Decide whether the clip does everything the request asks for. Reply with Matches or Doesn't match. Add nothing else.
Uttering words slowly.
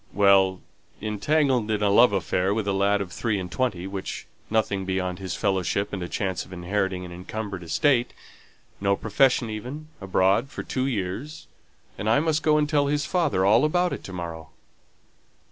Doesn't match